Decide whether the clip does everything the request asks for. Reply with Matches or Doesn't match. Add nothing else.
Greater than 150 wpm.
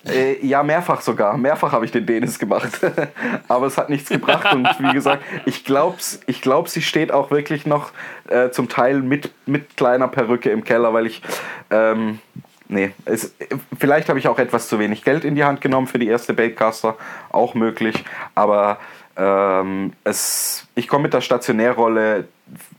Matches